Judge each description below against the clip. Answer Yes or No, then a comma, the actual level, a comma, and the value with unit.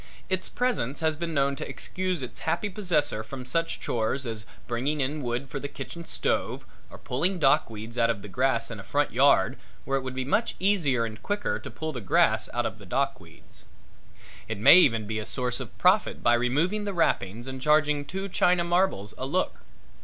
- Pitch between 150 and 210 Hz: No, medium, 140 Hz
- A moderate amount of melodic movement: No, wide, 6.3 semitones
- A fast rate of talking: Yes, fast, 210 wpm